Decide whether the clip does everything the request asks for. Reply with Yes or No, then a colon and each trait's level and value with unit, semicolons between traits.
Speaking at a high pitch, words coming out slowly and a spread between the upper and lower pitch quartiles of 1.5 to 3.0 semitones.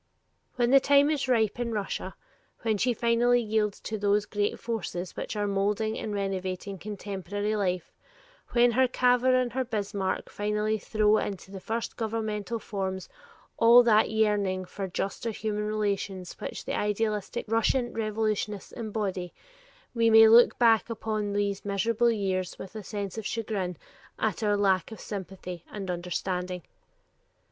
No: high, 210 Hz; average, 150 wpm; narrow, 2.5 semitones